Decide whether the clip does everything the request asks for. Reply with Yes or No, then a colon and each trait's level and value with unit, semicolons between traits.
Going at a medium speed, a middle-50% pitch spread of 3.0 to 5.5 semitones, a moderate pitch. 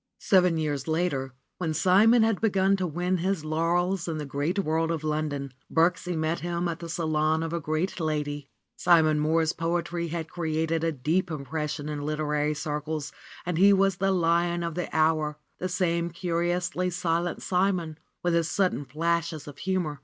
No: average, 170 wpm; narrow, 2.5 semitones; medium, 165 Hz